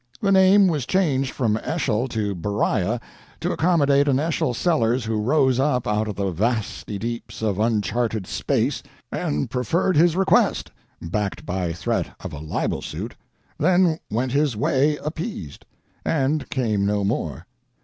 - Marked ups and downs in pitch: Yes, wide, 6.4 semitones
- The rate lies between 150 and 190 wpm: No, average, 140 wpm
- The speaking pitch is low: Yes, low, 120 Hz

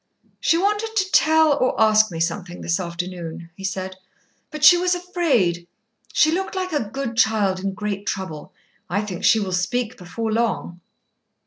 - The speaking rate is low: No, average, 165 wpm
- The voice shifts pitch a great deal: Yes, wide, 8.9 semitones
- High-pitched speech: Yes, high, 215 Hz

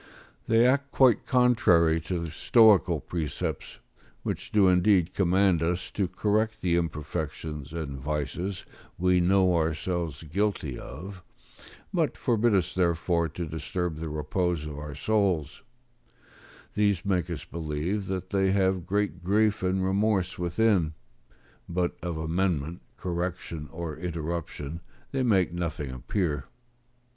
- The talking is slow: Yes, slow, 125 wpm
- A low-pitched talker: Yes, very low, 90 Hz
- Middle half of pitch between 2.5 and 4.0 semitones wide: Yes, average, 3.4 semitones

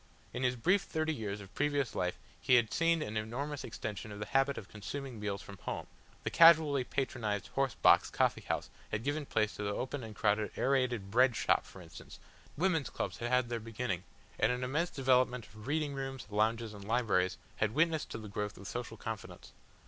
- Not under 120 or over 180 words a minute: No, average, 200 wpm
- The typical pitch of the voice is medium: No, low, 120 Hz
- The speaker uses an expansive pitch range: No, average, 4.6 semitones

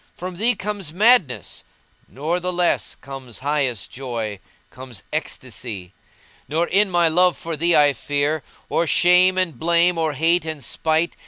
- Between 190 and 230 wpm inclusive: No, average, 160 wpm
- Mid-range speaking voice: Yes, medium, 160 Hz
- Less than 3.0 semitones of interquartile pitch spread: No, average, 4.6 semitones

